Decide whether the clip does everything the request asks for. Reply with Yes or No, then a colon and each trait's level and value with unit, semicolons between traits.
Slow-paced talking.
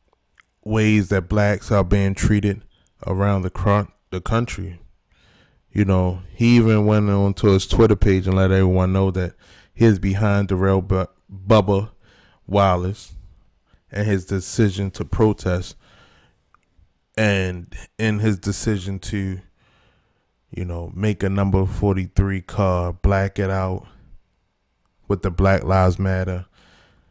Yes: slow, 130 wpm